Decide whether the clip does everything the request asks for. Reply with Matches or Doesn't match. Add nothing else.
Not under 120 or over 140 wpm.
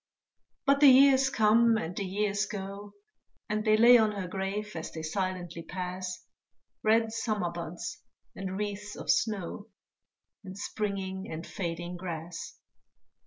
Matches